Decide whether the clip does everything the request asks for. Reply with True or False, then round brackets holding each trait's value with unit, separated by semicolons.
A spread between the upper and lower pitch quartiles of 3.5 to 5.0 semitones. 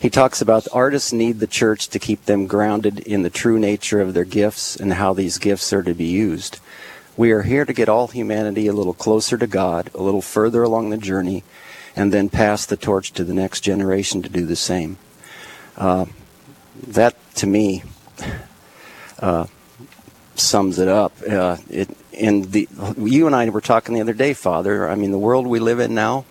False (3.1 semitones)